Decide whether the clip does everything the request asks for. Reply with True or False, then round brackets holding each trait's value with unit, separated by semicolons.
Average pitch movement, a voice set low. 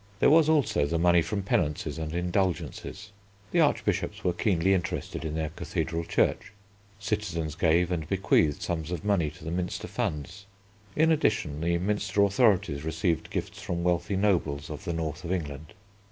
True (3.7 semitones; 85 Hz)